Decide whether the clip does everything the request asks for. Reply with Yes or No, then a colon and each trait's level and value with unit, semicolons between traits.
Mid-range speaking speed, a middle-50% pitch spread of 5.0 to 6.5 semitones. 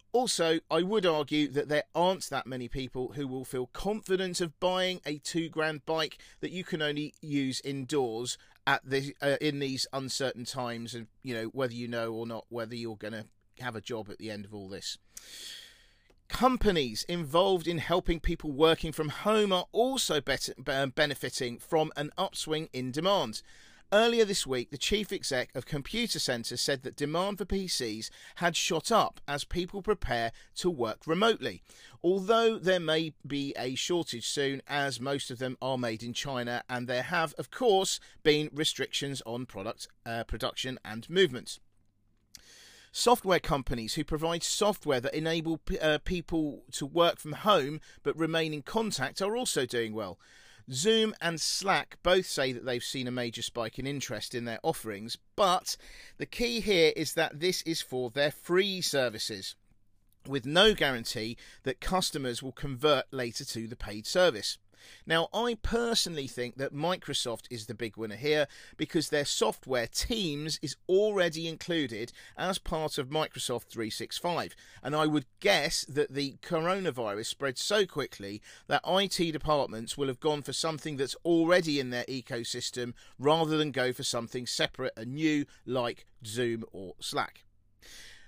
Yes: average, 165 wpm; wide, 5.4 semitones